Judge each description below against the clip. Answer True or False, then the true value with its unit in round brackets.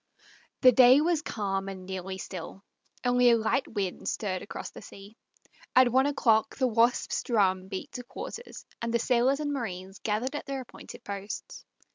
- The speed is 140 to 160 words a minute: False (170 wpm)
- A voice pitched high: True (230 Hz)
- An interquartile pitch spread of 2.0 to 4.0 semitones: False (4.8 semitones)